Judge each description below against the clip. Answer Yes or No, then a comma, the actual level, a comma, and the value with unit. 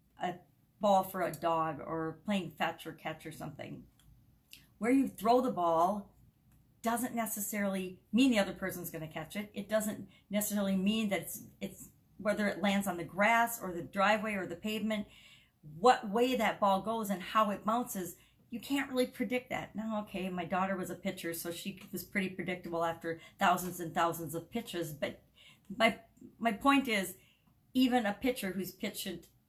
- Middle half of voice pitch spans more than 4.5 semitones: No, average, 4.1 semitones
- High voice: Yes, high, 195 Hz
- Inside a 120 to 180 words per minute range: Yes, average, 175 wpm